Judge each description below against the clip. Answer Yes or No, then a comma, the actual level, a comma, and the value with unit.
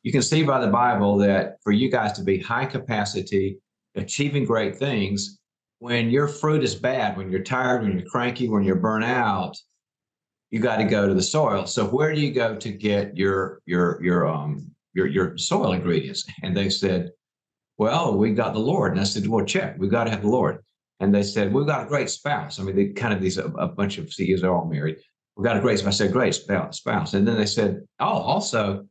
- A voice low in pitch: Yes, low, 100 Hz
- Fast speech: Yes, fast, 230 wpm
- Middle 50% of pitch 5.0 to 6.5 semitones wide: No, average, 4.0 semitones